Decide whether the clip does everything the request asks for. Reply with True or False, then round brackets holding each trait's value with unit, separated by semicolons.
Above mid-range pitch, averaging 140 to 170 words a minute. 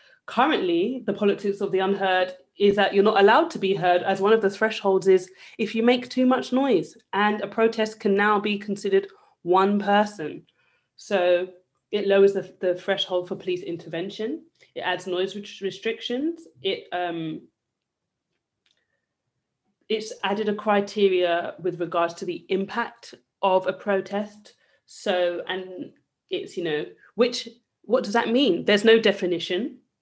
True (200 Hz; 150 wpm)